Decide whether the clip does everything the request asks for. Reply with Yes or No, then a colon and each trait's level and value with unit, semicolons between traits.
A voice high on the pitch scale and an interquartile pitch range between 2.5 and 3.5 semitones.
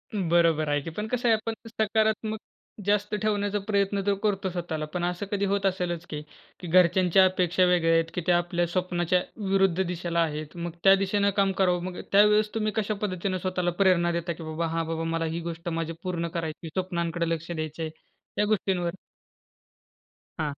No: medium, 180 Hz; average, 2.9 semitones